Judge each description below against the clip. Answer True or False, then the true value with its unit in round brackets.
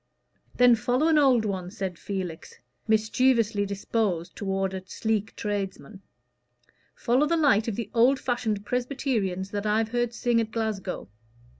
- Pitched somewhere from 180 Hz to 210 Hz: False (220 Hz)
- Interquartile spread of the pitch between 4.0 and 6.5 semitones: False (3.6 semitones)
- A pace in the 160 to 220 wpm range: False (140 wpm)